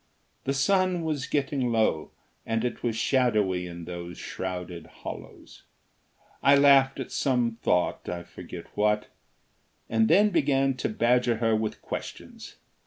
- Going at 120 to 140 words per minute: Yes, slow, 135 wpm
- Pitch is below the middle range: Yes, low, 120 Hz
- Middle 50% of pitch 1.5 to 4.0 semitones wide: No, average, 4.8 semitones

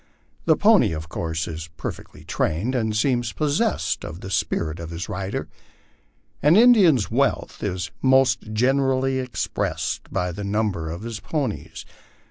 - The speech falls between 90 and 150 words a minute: Yes, average, 140 wpm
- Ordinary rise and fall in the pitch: No, wide, 7.9 semitones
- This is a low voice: Yes, low, 110 Hz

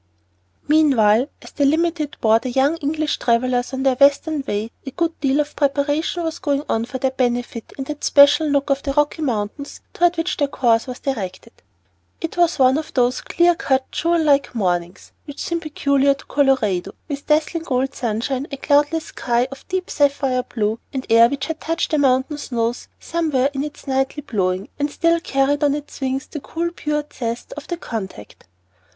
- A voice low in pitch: No, very high, 275 Hz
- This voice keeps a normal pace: Yes, average, 185 wpm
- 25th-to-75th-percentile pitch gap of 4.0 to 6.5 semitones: No, average, 3.3 semitones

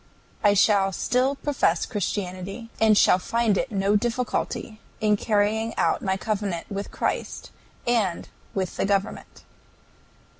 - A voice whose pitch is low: No, high, 205 Hz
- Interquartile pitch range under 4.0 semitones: Yes, average, 2.8 semitones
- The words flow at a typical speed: No, slow, 120 wpm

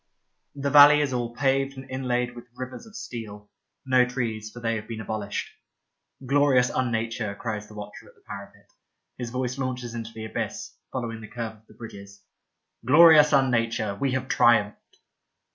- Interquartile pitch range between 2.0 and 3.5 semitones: Yes, average, 3.1 semitones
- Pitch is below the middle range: Yes, low, 120 Hz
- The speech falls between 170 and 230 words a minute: Yes, average, 175 wpm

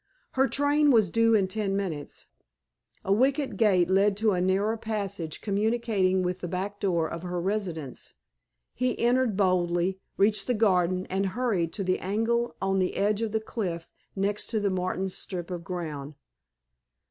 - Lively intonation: No, average, 3.3 semitones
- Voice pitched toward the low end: No, high, 195 Hz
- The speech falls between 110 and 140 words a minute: No, average, 165 wpm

